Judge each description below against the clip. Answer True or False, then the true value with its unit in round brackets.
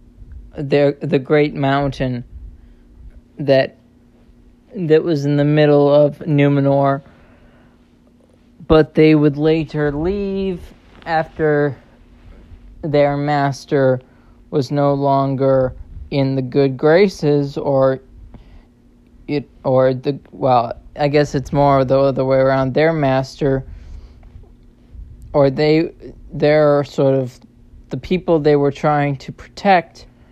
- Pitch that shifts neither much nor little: False (2.2 semitones)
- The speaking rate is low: True (105 wpm)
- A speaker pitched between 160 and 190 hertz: False (140 Hz)